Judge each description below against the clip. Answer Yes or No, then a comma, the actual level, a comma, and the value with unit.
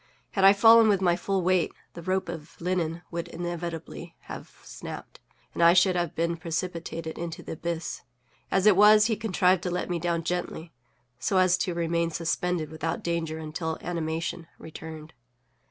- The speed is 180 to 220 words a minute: No, average, 170 wpm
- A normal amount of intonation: No, narrow, 2.0 semitones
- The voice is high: No, medium, 170 Hz